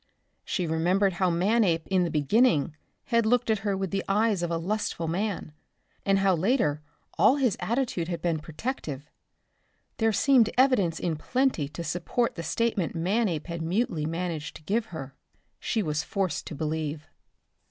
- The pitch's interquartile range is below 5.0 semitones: No, average, 5.3 semitones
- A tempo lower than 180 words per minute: Yes, average, 165 wpm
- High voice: No, medium, 180 Hz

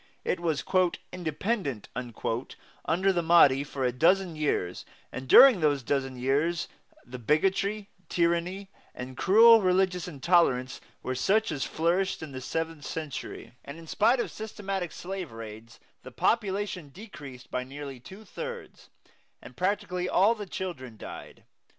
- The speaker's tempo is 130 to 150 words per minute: Yes, average, 140 wpm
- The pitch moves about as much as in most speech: No, wide, 6.3 semitones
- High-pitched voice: No, medium, 170 Hz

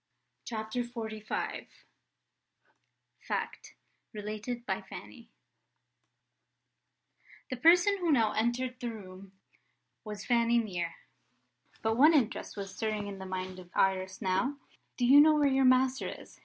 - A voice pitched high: Yes, high, 225 Hz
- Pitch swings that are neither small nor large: Yes, average, 4.2 semitones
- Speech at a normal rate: No, slow, 125 wpm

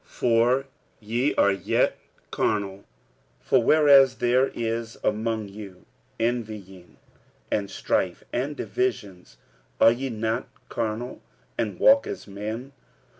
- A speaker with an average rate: No, slow, 115 wpm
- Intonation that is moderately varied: Yes, average, 3.4 semitones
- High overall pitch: No, low, 115 Hz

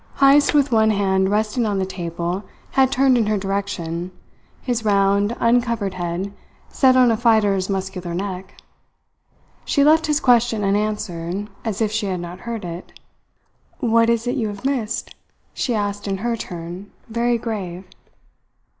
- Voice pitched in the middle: No, high, 210 Hz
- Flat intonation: No, average, 3.6 semitones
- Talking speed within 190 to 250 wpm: No, average, 155 wpm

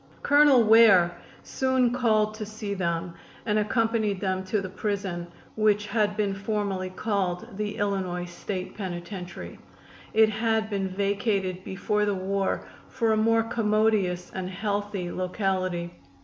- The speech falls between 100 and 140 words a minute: Yes, slow, 135 wpm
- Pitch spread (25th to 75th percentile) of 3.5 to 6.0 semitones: No, average, 2.7 semitones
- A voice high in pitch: Yes, high, 205 Hz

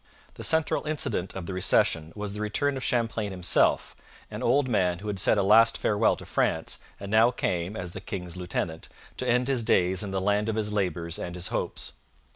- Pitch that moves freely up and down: No, average, 3.9 semitones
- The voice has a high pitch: No, low, 105 Hz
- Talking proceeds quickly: Yes, fast, 210 wpm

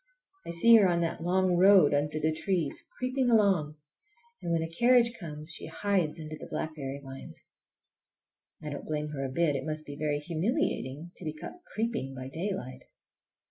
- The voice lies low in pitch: No, medium, 160 Hz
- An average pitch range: Yes, average, 4.4 semitones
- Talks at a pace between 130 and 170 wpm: No, average, 180 wpm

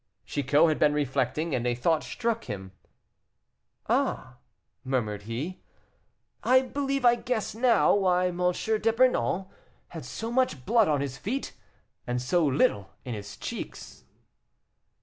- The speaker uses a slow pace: Yes, slow, 130 wpm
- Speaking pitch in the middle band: Yes, medium, 165 Hz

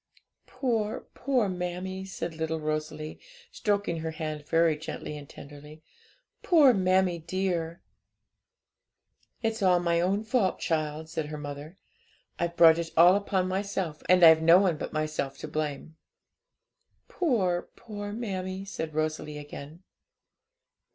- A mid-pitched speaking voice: Yes, medium, 170 Hz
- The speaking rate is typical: No, slow, 130 wpm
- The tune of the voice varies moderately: Yes, average, 3.7 semitones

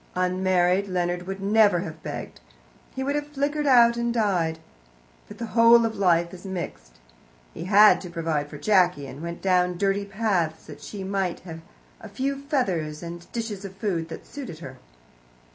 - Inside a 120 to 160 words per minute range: No, average, 175 wpm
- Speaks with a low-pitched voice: No, high, 190 Hz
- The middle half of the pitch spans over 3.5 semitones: Yes, average, 4.6 semitones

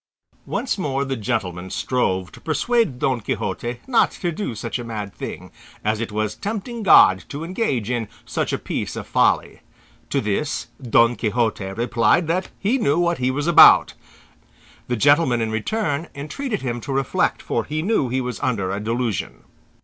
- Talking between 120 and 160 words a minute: No, average, 170 wpm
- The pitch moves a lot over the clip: Yes, wide, 6.7 semitones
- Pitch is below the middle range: Yes, low, 125 Hz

